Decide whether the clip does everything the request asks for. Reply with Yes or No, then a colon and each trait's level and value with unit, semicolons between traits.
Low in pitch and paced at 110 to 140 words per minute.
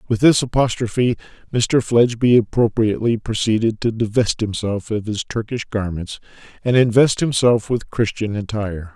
Yes: low, 110 Hz; slow, 135 wpm